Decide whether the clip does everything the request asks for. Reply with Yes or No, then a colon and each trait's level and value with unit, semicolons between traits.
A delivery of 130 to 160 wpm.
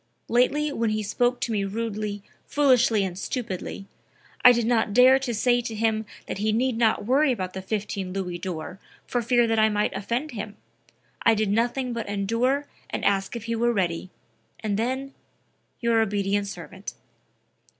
No: average, 170 wpm